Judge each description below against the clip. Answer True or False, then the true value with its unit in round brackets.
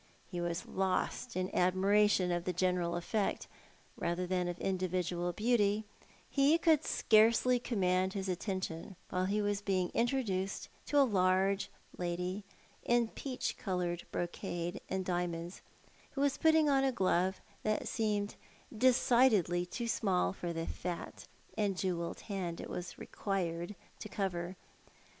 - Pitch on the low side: False (190 Hz)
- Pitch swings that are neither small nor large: True (3.2 semitones)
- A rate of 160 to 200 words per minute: False (145 wpm)